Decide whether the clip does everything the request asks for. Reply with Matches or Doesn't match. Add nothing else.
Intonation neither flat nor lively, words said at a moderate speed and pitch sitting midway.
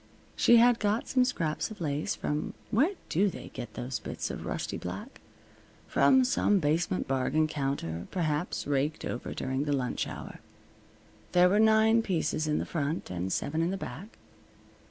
Doesn't match